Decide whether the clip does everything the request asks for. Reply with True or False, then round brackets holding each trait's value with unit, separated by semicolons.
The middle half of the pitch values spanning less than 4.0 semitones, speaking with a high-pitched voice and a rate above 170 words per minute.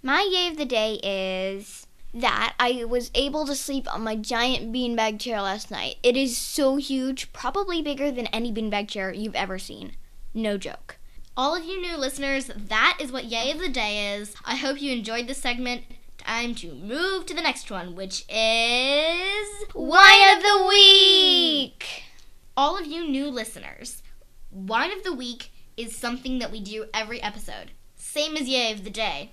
False (5.3 semitones; 250 Hz; 180 wpm)